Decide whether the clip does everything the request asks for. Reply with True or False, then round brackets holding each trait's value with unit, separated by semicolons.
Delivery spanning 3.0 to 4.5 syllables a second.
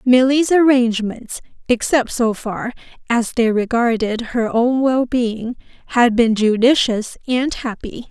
True (4.0 syllables/s)